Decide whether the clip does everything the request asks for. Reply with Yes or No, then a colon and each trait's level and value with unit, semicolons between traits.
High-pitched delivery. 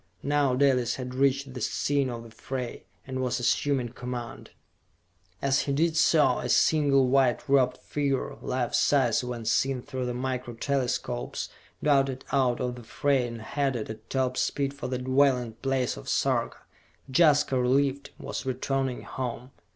No: low, 130 Hz